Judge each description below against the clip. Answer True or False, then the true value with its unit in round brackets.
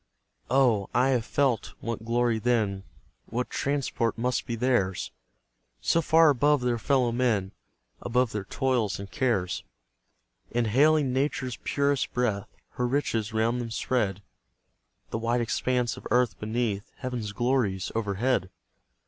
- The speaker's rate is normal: False (130 wpm)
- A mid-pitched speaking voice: False (120 Hz)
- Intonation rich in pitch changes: False (2.8 semitones)